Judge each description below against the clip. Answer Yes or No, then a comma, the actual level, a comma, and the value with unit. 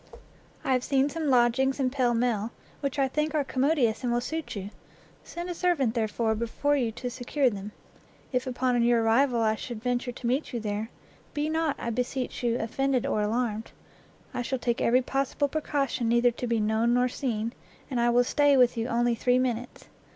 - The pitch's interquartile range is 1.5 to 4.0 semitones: Yes, narrow, 2.6 semitones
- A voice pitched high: Yes, high, 245 Hz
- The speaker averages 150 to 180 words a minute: No, average, 195 wpm